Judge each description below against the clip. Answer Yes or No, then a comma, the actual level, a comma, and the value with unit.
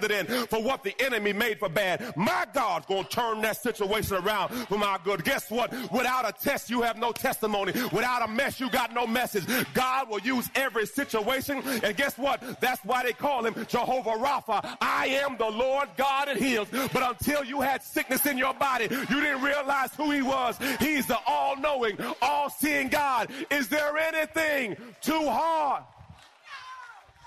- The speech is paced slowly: No, average, 175 wpm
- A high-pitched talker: Yes, very high, 255 Hz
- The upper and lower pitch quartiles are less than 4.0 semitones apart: Yes, average, 3.5 semitones